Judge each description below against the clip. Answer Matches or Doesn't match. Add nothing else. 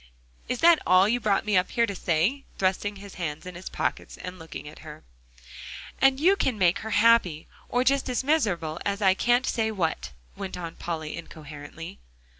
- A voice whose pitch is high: Matches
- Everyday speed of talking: Matches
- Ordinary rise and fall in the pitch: Doesn't match